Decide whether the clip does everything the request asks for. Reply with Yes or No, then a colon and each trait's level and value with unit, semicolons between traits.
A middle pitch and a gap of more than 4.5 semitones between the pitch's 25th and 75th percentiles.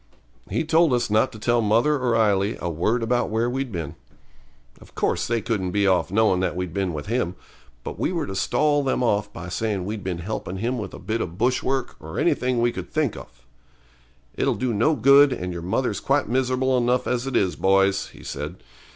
No: low, 110 Hz; average, 5.0 semitones